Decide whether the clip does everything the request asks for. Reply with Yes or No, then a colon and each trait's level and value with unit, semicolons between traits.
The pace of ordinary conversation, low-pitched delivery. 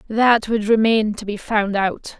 No: average, 190 wpm; high, 215 Hz